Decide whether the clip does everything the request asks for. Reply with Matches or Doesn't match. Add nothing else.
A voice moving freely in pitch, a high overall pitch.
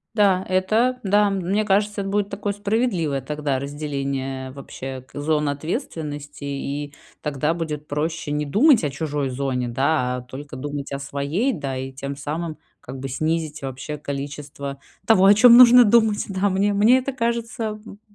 Doesn't match